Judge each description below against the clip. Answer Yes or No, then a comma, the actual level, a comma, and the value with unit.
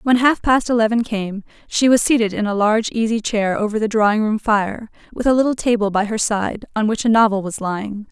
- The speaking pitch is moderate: No, high, 220 Hz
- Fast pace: Yes, fast, 230 wpm